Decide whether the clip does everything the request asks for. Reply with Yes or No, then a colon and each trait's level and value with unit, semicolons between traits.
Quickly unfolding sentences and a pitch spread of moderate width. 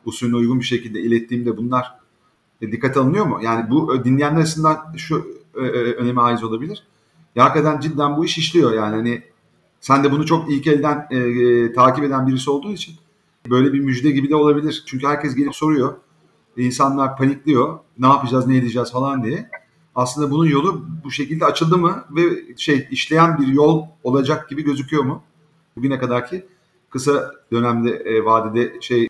Yes: fast, 170 wpm; average, 3.9 semitones